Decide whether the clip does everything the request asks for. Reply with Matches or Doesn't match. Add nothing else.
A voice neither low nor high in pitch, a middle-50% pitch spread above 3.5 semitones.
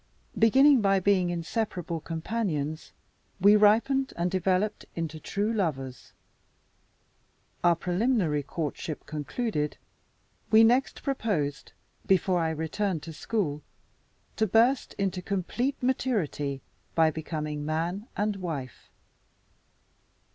Matches